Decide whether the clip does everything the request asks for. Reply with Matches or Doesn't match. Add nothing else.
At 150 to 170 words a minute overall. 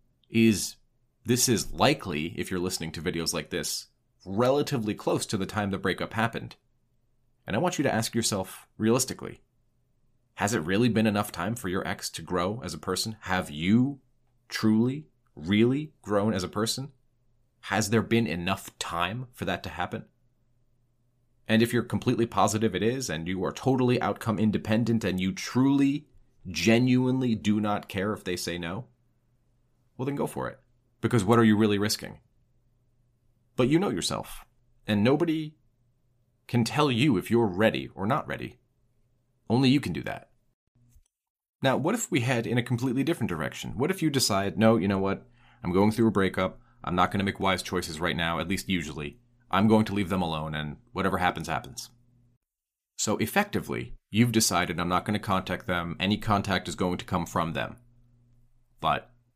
Doesn't match